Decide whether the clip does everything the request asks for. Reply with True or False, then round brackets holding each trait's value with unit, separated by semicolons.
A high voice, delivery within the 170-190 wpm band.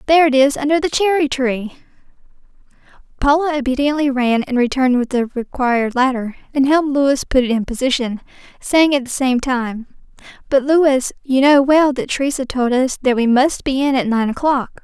True (265 Hz; 180 wpm)